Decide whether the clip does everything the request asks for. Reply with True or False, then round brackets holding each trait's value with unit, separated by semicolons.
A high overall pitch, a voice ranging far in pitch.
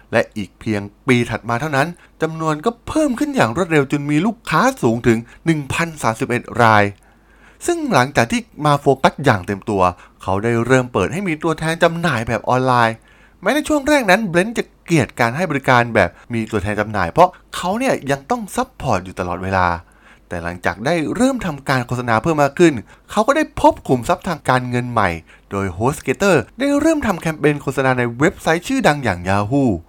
False (135 Hz; 7.7 semitones)